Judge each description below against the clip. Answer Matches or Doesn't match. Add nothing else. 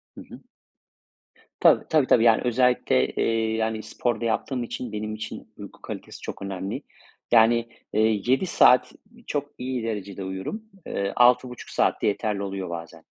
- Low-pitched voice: Matches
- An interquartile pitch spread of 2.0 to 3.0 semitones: Doesn't match